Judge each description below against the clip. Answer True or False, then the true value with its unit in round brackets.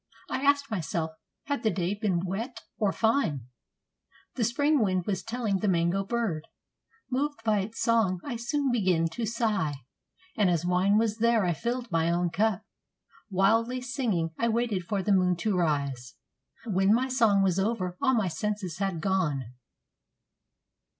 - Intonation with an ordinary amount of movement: True (4.6 semitones)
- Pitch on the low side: False (205 Hz)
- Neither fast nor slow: True (160 wpm)